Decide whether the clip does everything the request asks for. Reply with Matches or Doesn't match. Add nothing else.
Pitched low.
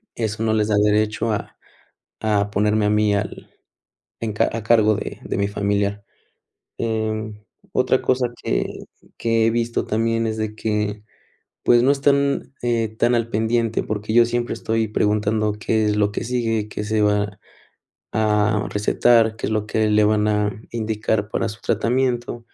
Matches